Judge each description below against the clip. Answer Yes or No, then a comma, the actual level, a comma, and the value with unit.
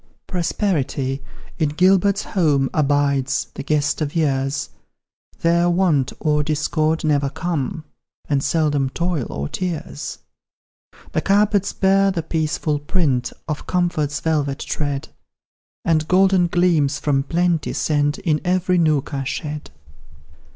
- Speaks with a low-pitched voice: No, medium, 155 Hz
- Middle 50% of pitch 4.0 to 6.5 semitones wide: No, average, 3.5 semitones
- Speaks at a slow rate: Yes, slow, 120 wpm